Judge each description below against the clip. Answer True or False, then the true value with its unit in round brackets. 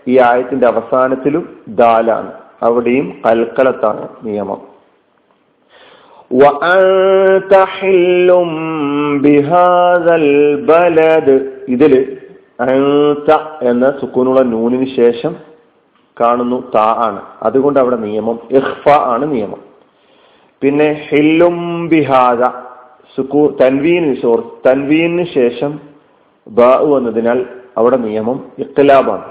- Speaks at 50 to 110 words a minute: True (65 wpm)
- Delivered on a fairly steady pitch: False (4.5 semitones)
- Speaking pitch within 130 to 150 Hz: True (135 Hz)